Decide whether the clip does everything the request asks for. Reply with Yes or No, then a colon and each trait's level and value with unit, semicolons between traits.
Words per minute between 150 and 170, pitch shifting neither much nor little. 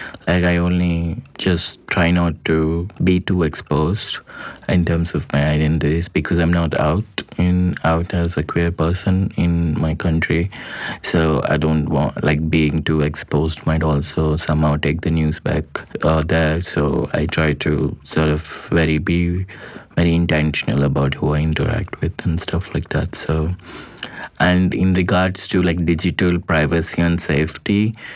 No: average, 160 wpm; narrow, 2.2 semitones